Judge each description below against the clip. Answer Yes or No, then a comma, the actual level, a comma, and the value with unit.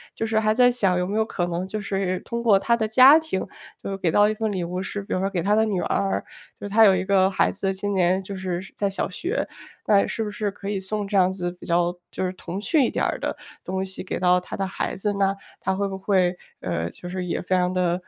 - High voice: Yes, high, 195 Hz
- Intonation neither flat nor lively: No, narrow, 2.3 semitones